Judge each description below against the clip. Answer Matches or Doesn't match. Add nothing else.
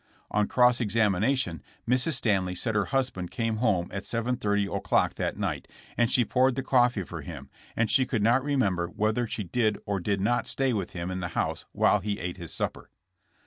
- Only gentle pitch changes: Doesn't match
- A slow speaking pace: Doesn't match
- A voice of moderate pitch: Doesn't match